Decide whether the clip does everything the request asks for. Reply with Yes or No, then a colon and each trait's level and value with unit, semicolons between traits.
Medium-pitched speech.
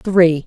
Yes: medium, 170 Hz